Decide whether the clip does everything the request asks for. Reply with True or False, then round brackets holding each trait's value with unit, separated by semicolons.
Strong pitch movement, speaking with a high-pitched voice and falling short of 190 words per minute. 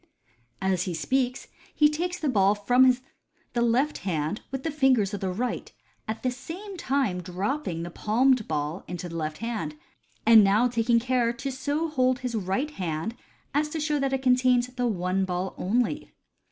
True (5.9 semitones; 240 Hz; 180 wpm)